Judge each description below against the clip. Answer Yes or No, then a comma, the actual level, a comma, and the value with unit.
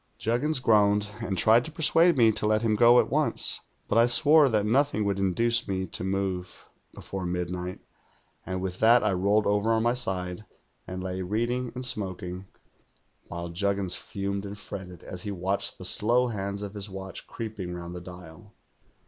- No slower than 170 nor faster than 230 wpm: Yes, average, 180 wpm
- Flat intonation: No, average, 3.6 semitones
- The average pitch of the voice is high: No, low, 100 Hz